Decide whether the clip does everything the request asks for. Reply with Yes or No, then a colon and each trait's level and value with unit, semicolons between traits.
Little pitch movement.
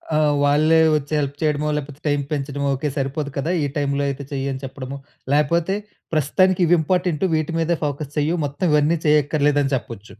Yes: narrow, 1.9 semitones